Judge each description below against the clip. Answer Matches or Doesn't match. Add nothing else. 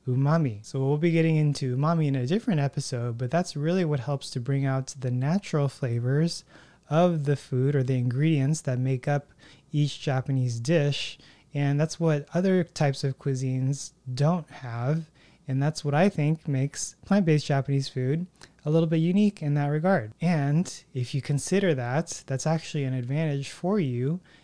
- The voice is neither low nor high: Matches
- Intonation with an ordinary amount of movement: Matches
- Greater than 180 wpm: Doesn't match